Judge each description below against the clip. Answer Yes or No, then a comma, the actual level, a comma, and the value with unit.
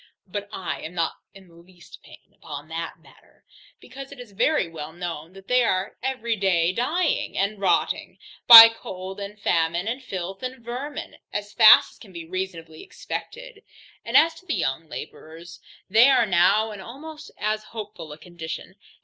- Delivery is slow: No, average, 175 wpm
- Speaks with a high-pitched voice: Yes, high, 195 Hz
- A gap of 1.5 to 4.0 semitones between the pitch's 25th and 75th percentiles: No, wide, 5.4 semitones